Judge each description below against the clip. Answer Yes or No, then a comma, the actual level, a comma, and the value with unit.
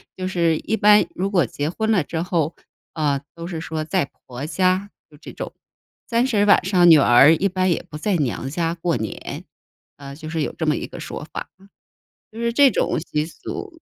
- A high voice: No, medium, 170 Hz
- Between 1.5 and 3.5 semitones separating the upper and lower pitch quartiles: No, average, 4.1 semitones